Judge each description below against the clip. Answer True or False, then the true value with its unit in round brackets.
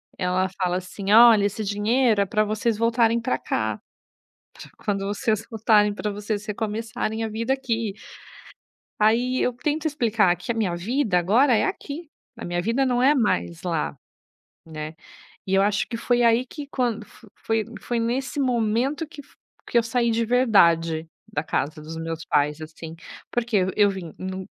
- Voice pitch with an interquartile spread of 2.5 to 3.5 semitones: False (4.1 semitones)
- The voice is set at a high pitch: True (220 Hz)